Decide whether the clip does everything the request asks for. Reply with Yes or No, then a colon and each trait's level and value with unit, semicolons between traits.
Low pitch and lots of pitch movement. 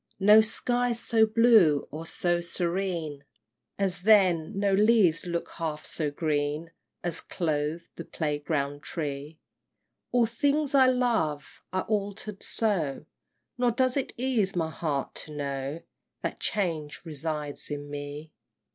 No: medium, 170 Hz; wide, 6.2 semitones